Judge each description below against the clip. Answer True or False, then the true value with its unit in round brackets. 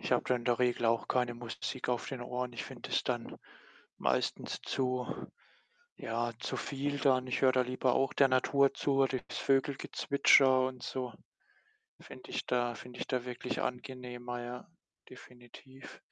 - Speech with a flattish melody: True (1.3 semitones)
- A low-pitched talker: True (125 Hz)